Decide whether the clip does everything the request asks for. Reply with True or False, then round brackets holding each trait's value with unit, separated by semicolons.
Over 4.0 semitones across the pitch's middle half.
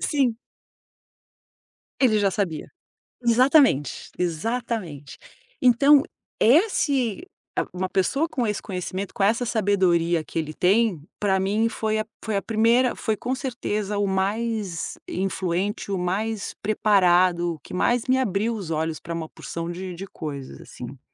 True (4.6 semitones)